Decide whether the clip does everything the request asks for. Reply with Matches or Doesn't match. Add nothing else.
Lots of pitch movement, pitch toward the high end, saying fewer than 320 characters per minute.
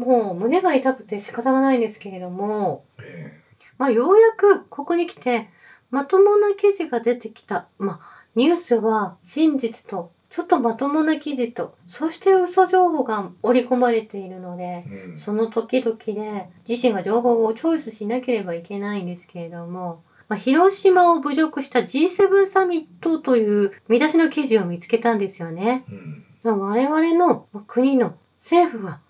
Matches